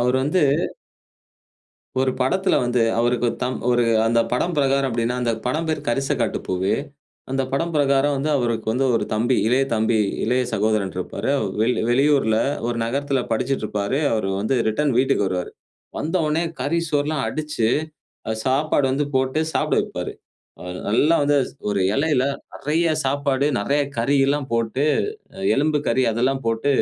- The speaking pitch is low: Yes, low, 130 Hz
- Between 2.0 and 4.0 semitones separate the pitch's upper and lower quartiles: Yes, average, 3.7 semitones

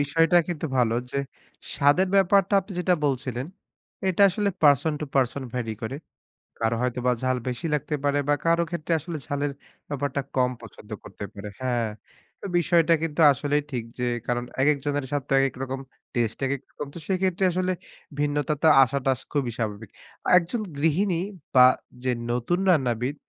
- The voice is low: No, medium, 145 Hz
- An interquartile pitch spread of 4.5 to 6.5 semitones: Yes, average, 4.8 semitones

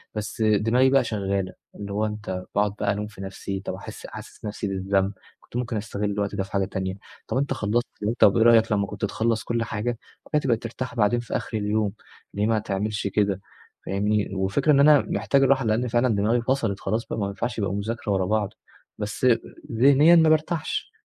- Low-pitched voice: Yes, low, 105 Hz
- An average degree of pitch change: Yes, average, 3.0 semitones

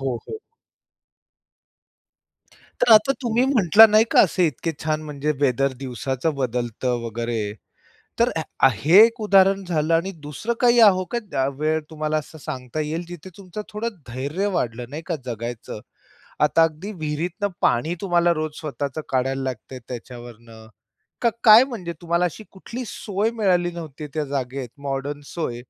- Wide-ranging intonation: Yes, wide, 6.5 semitones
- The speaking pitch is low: No, medium, 155 Hz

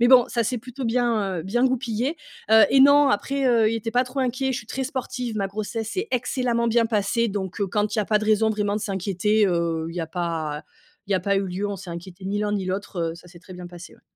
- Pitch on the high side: Yes, high, 215 Hz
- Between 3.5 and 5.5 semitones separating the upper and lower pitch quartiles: Yes, average, 4.1 semitones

